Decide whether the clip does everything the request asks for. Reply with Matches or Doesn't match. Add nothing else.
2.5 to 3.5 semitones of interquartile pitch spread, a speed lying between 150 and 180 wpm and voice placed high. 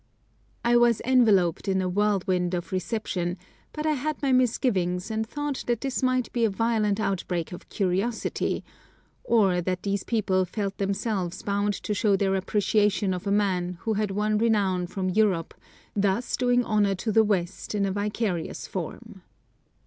Matches